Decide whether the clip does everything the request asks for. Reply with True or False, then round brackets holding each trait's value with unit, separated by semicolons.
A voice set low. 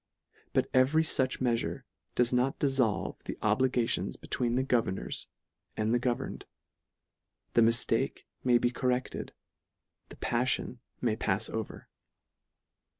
True (125 Hz)